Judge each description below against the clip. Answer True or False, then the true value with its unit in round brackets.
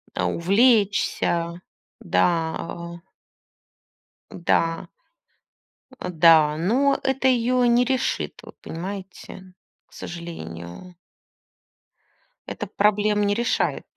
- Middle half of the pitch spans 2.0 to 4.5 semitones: False (5.5 semitones)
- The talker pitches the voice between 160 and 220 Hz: True (190 Hz)